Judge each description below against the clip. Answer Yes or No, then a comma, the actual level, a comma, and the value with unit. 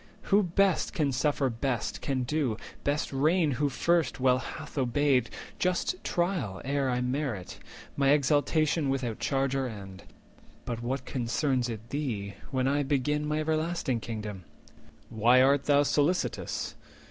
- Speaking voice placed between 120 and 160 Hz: Yes, low, 135 Hz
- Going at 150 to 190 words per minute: No, slow, 135 wpm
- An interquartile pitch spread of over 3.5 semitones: No, average, 3.2 semitones